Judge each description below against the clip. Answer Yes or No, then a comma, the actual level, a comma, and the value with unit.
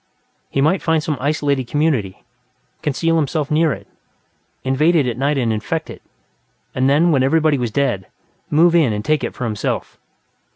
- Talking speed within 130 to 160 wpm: No, average, 170 wpm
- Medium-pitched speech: Yes, medium, 145 Hz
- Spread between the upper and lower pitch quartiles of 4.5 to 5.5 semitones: No, average, 3.7 semitones